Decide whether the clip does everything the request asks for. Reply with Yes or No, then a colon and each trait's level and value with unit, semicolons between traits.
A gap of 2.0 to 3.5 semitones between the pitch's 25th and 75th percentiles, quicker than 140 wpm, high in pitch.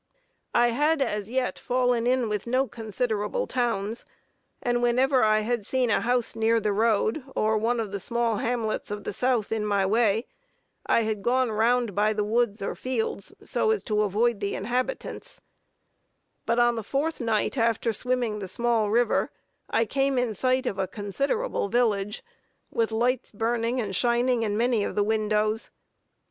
Yes: average, 2.7 semitones; average, 170 wpm; high, 230 Hz